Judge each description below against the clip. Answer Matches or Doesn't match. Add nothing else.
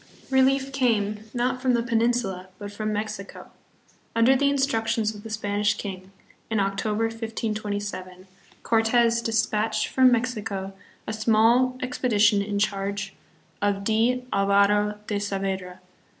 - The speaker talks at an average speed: Doesn't match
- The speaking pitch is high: Matches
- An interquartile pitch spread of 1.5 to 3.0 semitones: Matches